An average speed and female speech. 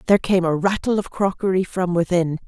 Yes: average, 195 wpm; female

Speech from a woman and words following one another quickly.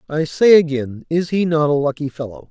No: male; fast, 215 wpm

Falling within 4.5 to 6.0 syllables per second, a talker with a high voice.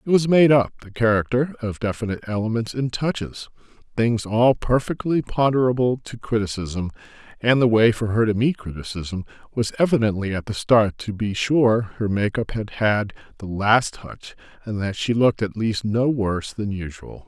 No: 4.9 syllables/s; low, 115 Hz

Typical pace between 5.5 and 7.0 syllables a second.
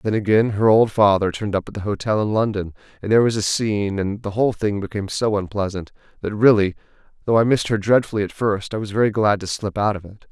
Yes: 6.6 syllables/s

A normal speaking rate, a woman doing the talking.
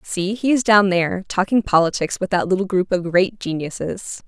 Yes: average, 195 wpm; female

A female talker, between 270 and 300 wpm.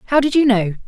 Yes: female; fast, 275 wpm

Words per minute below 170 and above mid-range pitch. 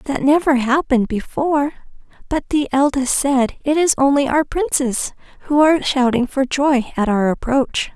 Yes: average, 160 wpm; very high, 270 Hz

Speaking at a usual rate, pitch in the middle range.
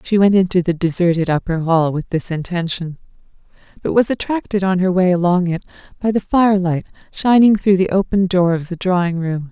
Yes: average, 190 wpm; medium, 180 Hz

